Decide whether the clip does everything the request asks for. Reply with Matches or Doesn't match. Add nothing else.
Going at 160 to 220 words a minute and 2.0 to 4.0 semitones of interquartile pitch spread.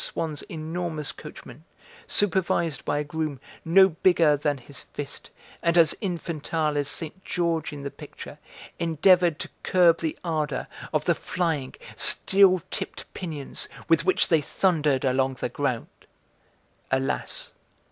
Doesn't match